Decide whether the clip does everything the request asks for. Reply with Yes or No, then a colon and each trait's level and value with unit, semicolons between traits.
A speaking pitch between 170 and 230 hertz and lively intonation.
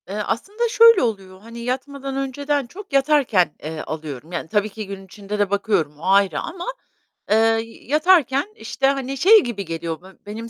Yes: high, 225 Hz; wide, 6.3 semitones